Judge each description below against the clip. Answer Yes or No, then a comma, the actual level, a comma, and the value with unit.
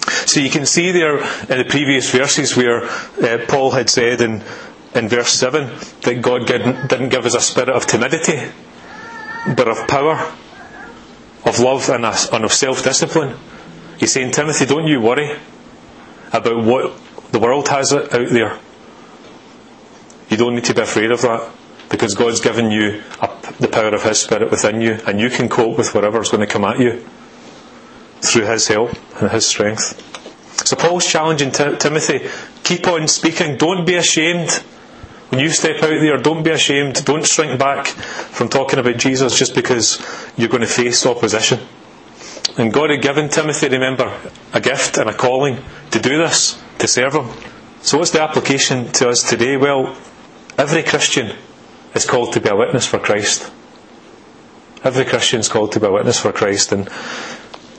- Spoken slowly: No, average, 170 wpm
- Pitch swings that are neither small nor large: Yes, average, 4.0 semitones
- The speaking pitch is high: No, low, 135 Hz